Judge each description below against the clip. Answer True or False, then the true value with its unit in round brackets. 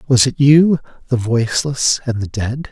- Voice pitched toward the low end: True (130 Hz)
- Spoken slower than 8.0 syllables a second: True (4.6 syllables/s)